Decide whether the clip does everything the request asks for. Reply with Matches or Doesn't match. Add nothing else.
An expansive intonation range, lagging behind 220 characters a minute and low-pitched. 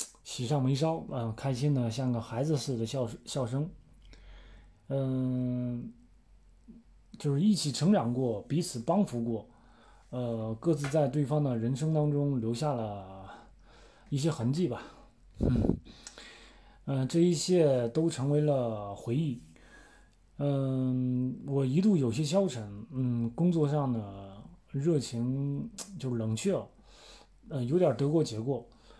Doesn't match